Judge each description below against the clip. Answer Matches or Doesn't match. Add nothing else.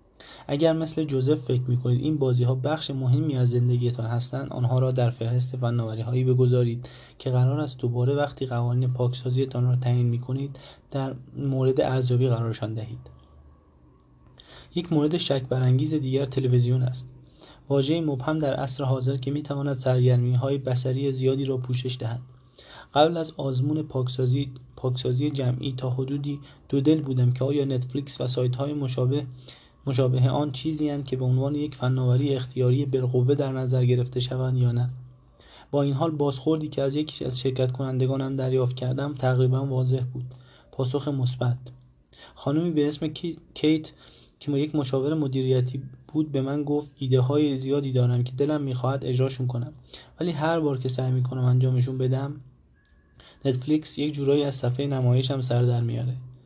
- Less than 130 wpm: Doesn't match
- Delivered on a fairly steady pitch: Matches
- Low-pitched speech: Matches